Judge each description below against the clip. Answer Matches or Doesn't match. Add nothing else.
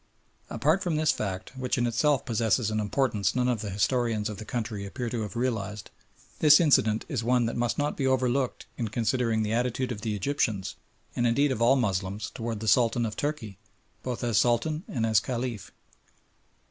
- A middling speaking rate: Matches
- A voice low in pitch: Matches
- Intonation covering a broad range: Doesn't match